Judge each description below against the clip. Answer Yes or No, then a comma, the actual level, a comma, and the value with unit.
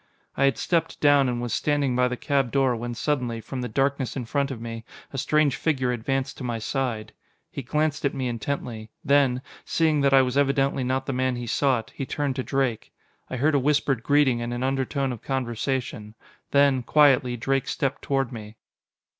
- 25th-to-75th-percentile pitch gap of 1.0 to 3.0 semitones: Yes, narrow, 2.5 semitones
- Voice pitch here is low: Yes, low, 130 Hz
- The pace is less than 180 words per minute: No, average, 195 wpm